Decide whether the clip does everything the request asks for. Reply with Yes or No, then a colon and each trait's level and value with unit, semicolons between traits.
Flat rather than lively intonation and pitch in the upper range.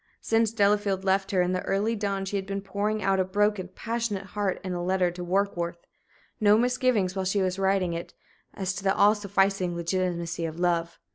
Yes: narrow, 2.1 semitones; high, 195 Hz